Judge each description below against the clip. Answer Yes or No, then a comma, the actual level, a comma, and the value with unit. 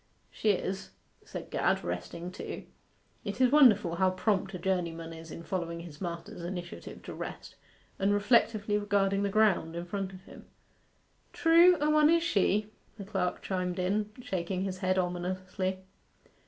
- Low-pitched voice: No, high, 190 Hz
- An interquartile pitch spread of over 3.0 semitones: No, narrow, 2.6 semitones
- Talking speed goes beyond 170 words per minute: No, average, 155 wpm